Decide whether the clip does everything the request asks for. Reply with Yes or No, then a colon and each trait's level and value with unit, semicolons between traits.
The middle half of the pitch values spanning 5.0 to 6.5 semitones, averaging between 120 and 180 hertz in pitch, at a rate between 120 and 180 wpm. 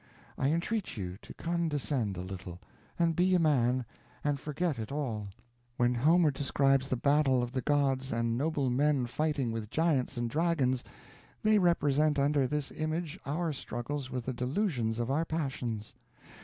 No: average, 4.2 semitones; medium, 140 Hz; average, 160 wpm